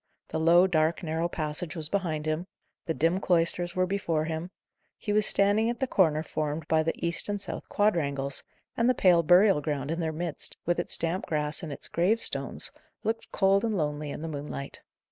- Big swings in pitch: No, average, 3.6 semitones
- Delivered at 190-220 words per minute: Yes, average, 195 wpm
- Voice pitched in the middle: Yes, medium, 170 Hz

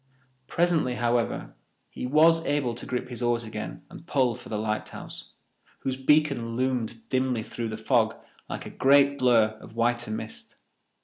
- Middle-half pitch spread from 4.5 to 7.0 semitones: No, average, 2.8 semitones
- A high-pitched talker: No, low, 125 Hz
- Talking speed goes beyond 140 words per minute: Yes, average, 160 wpm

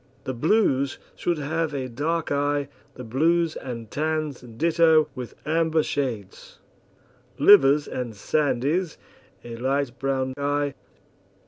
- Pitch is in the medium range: Yes, medium, 145 Hz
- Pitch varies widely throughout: No, average, 3.5 semitones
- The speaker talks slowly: Yes, slow, 115 wpm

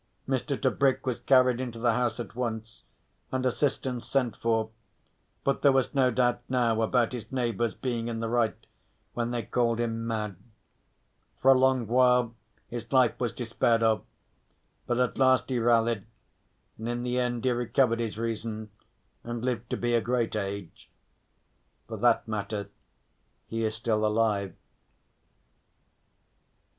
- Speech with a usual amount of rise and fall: No, narrow, 1.9 semitones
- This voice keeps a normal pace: Yes, average, 150 wpm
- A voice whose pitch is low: Yes, low, 120 Hz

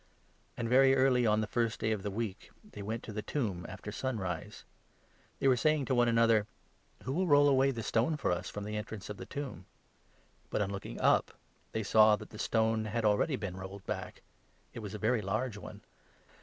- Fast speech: Yes, fast, 225 wpm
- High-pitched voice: No, low, 110 Hz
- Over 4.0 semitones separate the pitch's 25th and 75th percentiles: No, average, 3.7 semitones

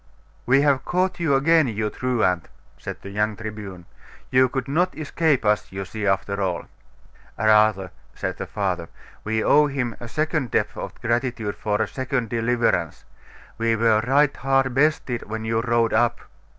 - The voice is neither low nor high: No, low, 115 Hz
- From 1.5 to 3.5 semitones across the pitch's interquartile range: No, average, 4.1 semitones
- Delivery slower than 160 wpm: No, average, 165 wpm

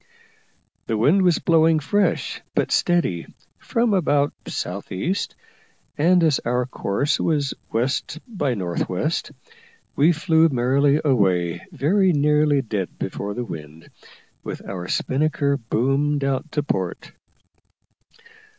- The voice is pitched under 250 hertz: Yes, medium, 140 Hz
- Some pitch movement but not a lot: No, wide, 5.9 semitones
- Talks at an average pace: No, slow, 115 wpm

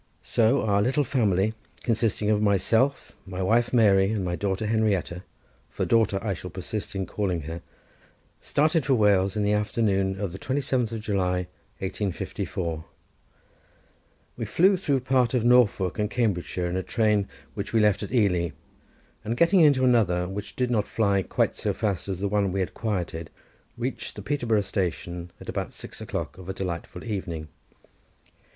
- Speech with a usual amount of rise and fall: Yes, average, 3.7 semitones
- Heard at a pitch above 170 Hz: No, low, 105 Hz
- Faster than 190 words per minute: No, average, 165 wpm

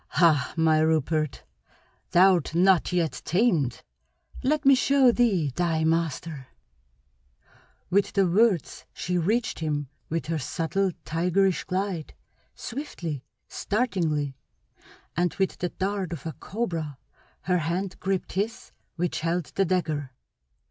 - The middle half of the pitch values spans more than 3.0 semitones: Yes, average, 3.6 semitones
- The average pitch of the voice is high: No, medium, 175 Hz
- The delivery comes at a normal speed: No, slow, 120 wpm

